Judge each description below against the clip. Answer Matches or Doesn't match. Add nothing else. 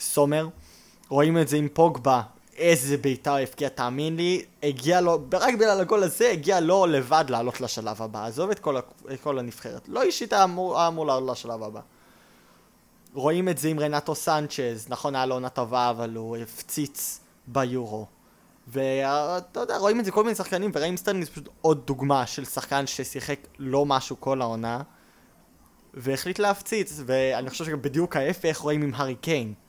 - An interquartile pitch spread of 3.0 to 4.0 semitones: Doesn't match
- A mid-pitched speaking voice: Matches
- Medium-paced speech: Doesn't match